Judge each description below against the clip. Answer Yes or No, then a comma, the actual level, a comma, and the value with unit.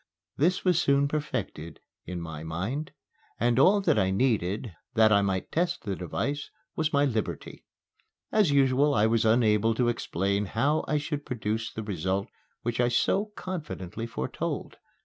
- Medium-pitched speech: No, low, 115 Hz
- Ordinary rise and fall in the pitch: No, wide, 6.5 semitones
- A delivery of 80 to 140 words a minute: No, average, 150 wpm